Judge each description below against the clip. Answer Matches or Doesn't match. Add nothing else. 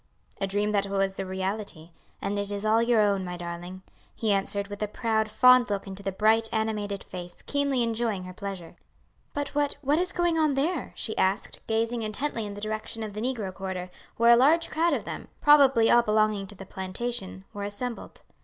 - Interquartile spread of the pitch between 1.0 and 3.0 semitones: Doesn't match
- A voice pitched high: Matches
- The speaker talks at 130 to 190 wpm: Doesn't match